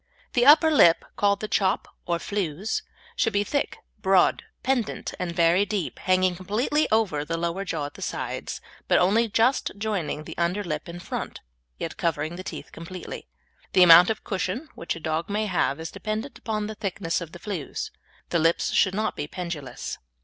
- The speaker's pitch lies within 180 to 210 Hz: Yes, medium, 185 Hz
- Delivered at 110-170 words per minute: No, average, 185 wpm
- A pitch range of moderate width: Yes, average, 4.1 semitones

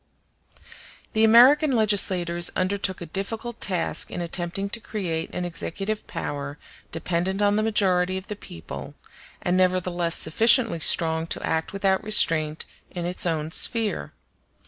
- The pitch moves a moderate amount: Yes, average, 3.7 semitones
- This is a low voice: No, medium, 185 Hz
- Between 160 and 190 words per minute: No, slow, 135 wpm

